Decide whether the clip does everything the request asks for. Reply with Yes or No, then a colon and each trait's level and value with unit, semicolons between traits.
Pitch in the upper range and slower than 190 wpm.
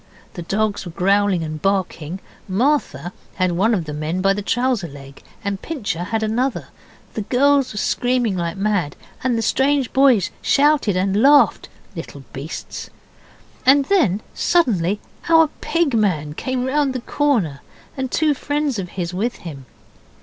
Yes: high, 210 Hz; average, 155 wpm